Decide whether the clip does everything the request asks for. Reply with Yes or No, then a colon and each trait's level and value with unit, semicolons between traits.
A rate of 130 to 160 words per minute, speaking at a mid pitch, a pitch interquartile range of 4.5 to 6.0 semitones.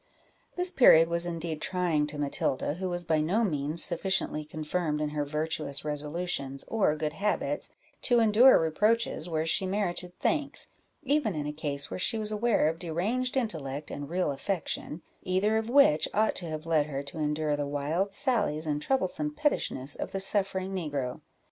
No: average, 175 wpm; medium, 165 Hz; wide, 5.4 semitones